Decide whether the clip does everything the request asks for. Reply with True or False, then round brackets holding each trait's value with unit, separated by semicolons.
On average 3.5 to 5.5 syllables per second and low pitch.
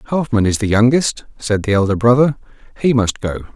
False (5.7 syllables/s; 115 Hz)